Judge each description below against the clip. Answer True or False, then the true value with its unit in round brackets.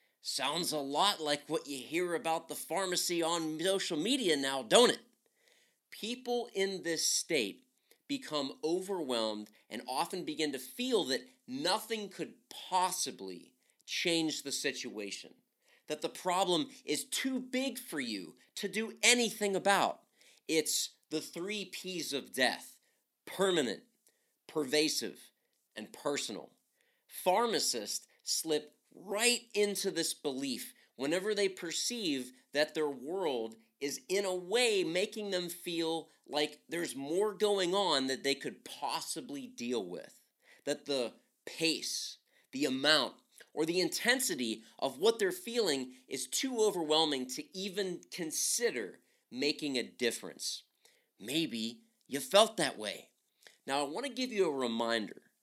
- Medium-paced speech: False (130 wpm)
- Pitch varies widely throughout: True (6.8 semitones)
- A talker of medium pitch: True (175 Hz)